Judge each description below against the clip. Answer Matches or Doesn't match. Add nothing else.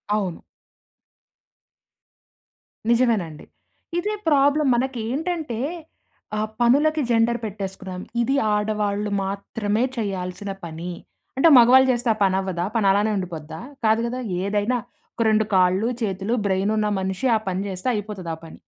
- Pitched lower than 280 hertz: Matches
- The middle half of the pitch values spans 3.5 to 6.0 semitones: Matches